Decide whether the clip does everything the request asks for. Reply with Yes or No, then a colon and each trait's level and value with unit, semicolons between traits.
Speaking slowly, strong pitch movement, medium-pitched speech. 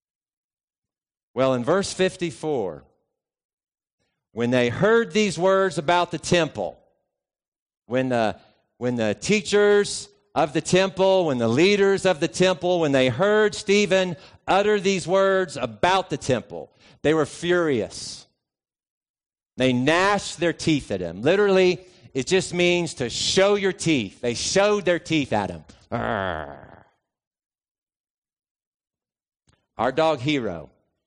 Yes: slow, 120 wpm; wide, 7.0 semitones; medium, 170 Hz